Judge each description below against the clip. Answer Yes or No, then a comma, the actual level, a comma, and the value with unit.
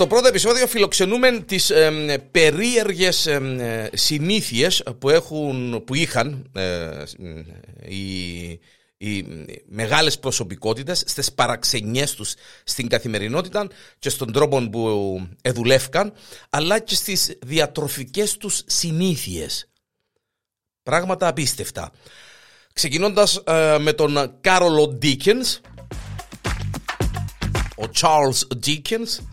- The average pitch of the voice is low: No, medium, 150 Hz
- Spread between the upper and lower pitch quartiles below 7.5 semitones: No, wide, 7.8 semitones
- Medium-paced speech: No, slow, 90 wpm